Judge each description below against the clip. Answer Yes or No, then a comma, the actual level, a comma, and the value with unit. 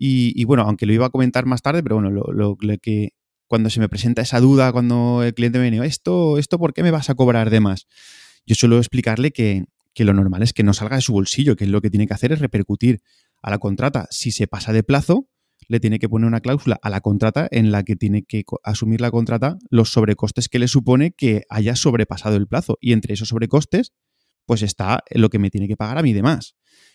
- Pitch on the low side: Yes, low, 115 Hz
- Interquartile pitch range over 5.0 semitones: No, average, 3.2 semitones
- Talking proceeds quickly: Yes, fast, 245 wpm